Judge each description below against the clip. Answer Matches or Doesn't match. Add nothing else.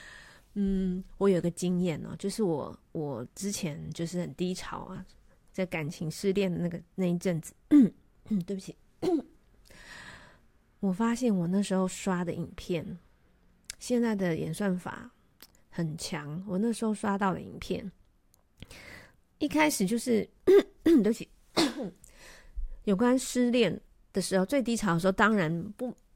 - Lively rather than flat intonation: Doesn't match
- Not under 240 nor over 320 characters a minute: Doesn't match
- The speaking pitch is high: Matches